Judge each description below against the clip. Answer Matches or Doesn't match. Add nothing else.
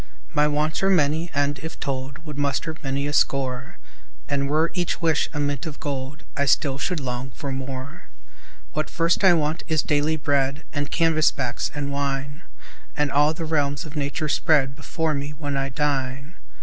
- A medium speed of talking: Matches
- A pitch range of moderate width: Doesn't match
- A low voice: Doesn't match